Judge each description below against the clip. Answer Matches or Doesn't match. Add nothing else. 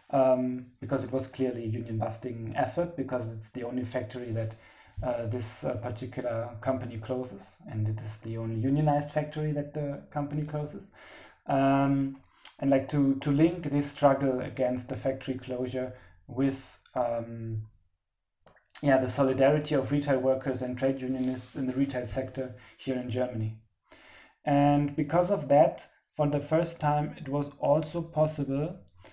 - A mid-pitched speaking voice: Doesn't match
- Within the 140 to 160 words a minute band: Matches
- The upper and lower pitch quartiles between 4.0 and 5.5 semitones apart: Doesn't match